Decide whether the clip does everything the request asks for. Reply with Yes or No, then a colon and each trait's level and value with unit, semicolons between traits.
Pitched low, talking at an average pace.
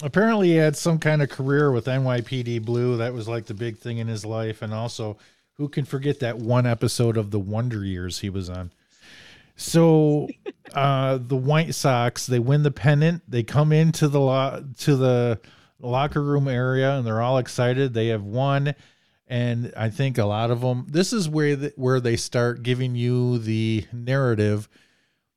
Yes: low, 125 Hz; average, 185 wpm